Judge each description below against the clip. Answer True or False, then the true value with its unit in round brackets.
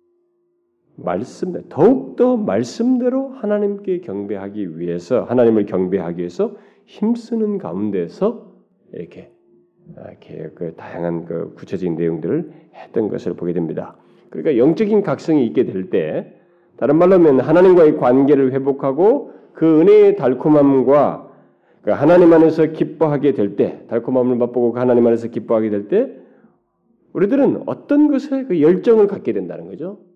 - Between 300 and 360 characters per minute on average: True (310 characters per minute)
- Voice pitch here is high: False (150 Hz)